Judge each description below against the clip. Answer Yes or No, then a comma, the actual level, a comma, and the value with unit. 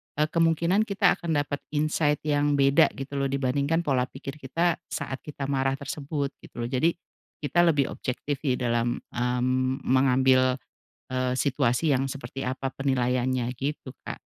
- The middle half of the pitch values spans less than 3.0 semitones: Yes, narrow, 2.4 semitones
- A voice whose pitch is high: No, low, 135 Hz